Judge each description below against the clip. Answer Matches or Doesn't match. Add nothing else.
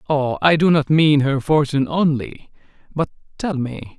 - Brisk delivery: Doesn't match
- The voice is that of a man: Matches